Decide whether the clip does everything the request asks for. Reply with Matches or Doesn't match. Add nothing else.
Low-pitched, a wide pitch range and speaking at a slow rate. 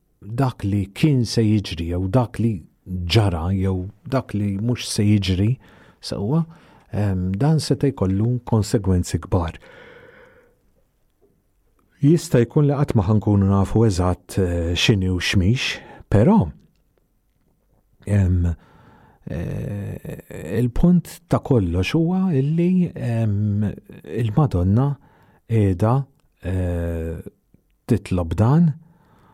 Matches